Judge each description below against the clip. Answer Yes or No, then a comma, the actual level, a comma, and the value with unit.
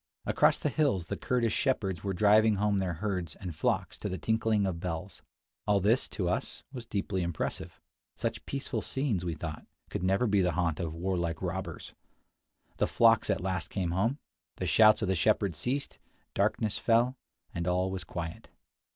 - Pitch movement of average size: Yes, average, 3.9 semitones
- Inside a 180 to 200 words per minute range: Yes, average, 185 wpm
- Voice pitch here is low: Yes, very low, 95 Hz